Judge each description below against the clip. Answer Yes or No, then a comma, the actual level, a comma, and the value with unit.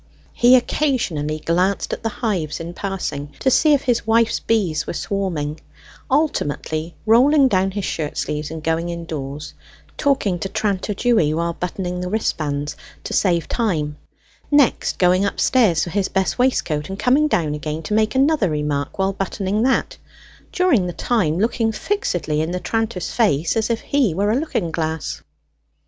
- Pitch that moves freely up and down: Yes, wide, 6.3 semitones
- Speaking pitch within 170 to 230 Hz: Yes, high, 190 Hz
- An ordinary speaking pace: Yes, average, 160 wpm